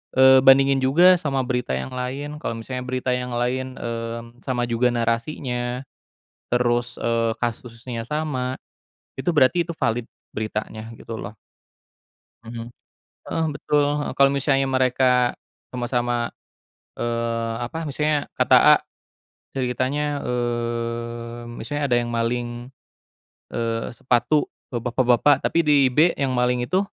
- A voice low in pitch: Yes, low, 125 Hz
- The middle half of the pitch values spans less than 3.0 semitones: Yes, narrow, 2.4 semitones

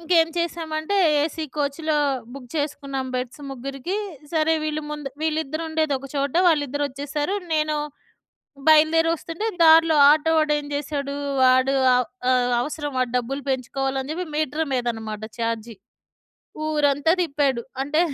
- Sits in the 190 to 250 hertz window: No, very high, 290 Hz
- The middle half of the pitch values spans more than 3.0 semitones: No, average, 2.7 semitones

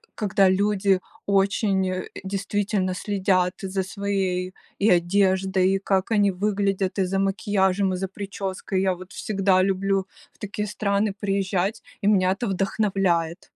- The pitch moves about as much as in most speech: No, narrow, 1.2 semitones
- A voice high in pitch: Yes, high, 195 Hz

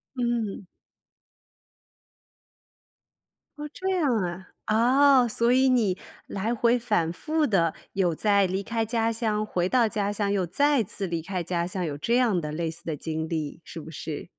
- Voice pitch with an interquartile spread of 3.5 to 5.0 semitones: No, wide, 5.6 semitones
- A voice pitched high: Yes, high, 205 Hz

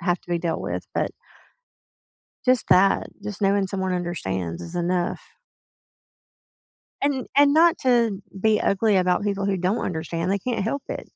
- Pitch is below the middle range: No, high, 195 Hz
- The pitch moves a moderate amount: Yes, average, 3.9 semitones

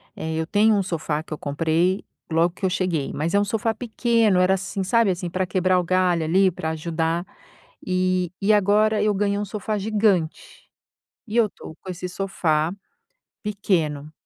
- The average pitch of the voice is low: No, medium, 185 Hz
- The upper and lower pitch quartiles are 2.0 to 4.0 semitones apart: Yes, average, 3.6 semitones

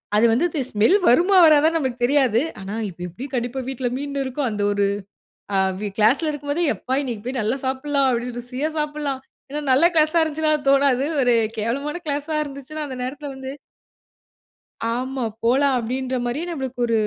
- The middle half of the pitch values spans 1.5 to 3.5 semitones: Yes, average, 3.2 semitones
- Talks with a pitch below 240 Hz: No, very high, 265 Hz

